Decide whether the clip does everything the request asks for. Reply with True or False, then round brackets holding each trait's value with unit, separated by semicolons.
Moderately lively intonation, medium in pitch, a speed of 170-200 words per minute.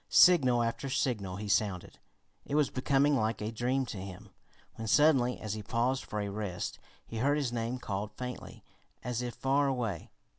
False (3.9 semitones; 120 Hz; 180 wpm)